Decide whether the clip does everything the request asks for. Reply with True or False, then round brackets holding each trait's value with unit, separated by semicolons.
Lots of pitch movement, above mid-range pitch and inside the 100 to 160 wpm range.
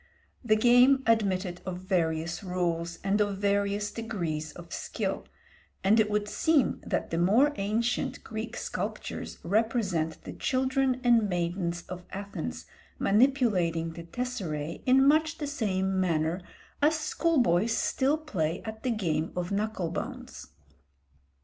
True (5.9 semitones; 200 Hz; 135 wpm)